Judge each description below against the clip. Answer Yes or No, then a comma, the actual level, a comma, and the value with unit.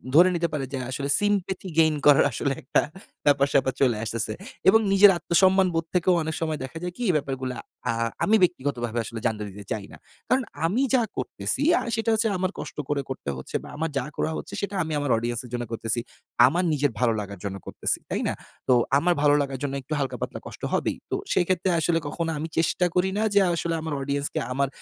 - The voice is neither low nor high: Yes, medium, 145 Hz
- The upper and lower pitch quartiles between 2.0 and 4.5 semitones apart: No, wide, 5.5 semitones